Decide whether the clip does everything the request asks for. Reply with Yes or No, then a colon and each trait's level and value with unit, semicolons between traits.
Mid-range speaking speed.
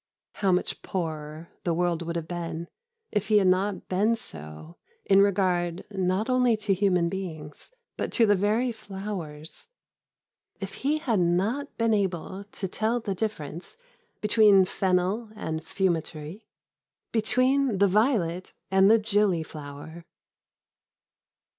No: slow, 130 wpm